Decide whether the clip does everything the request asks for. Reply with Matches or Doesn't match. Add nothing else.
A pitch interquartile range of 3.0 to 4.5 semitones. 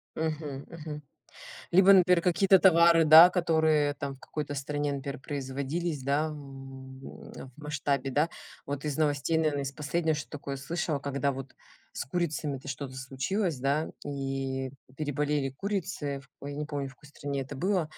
Doesn't match